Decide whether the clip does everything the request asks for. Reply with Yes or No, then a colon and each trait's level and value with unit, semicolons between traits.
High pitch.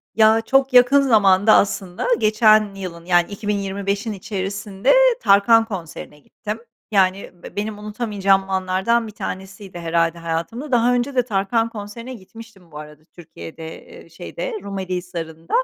Yes: high, 200 Hz